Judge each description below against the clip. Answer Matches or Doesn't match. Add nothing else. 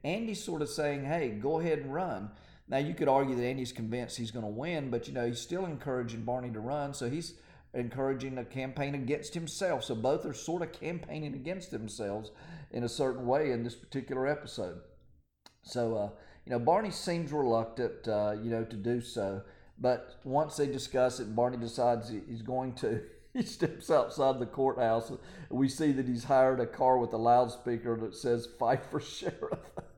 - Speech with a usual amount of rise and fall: Matches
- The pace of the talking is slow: Doesn't match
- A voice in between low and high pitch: Doesn't match